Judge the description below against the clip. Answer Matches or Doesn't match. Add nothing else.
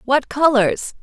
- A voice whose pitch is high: Matches